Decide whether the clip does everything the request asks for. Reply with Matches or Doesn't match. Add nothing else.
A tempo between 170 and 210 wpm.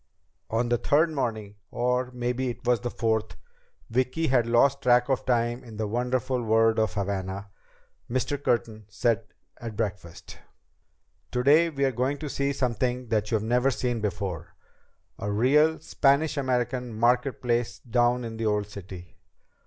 Doesn't match